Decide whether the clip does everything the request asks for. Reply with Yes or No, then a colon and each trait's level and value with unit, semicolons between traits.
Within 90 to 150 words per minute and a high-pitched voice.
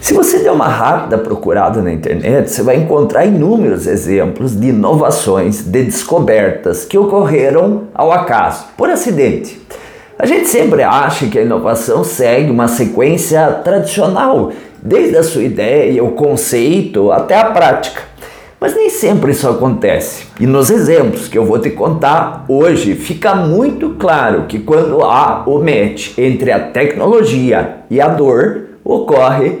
Yes: average, 145 wpm; high, 195 Hz